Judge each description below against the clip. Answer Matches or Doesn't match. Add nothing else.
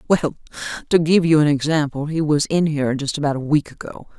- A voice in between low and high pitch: Matches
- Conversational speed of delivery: Doesn't match